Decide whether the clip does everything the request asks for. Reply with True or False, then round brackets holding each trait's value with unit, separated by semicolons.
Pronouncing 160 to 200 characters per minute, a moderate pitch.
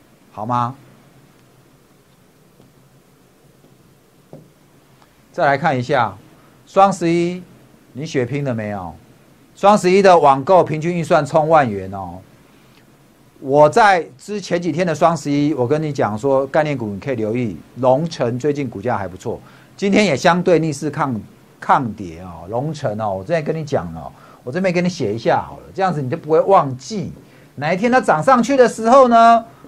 False (230 characters per minute; 145 Hz)